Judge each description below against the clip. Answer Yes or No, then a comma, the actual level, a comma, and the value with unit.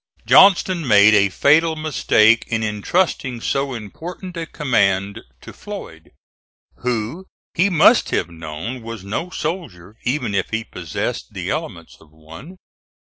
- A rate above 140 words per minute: No, slow, 135 wpm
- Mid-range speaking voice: No, low, 115 Hz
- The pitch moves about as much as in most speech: No, wide, 8.1 semitones